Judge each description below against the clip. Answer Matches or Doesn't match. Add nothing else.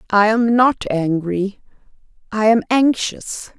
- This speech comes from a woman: Matches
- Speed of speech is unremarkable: Doesn't match